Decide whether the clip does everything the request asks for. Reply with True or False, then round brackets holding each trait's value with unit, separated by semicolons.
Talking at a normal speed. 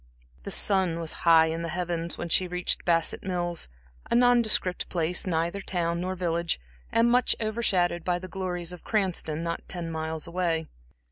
True (175 wpm)